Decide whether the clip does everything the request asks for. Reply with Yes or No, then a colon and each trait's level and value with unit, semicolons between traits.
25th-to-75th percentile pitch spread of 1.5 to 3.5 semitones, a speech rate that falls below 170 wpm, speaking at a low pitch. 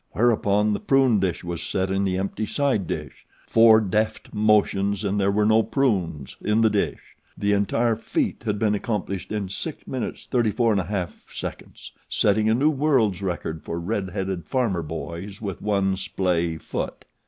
Yes: average, 2.8 semitones; average, 155 wpm; low, 100 Hz